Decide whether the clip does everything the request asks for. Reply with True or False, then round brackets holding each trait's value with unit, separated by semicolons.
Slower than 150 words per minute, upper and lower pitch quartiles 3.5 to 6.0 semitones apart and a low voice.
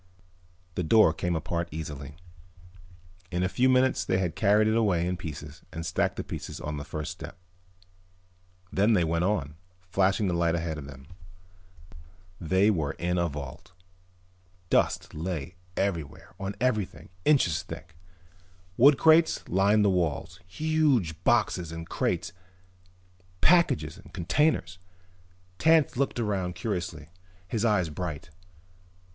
True (135 wpm; 4.8 semitones; 90 Hz)